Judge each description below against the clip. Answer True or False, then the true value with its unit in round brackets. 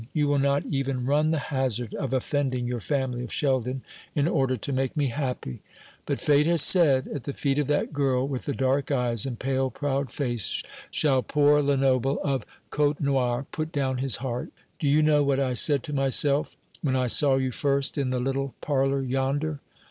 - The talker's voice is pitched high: False (135 Hz)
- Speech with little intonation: True (1.9 semitones)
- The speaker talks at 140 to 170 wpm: False (195 wpm)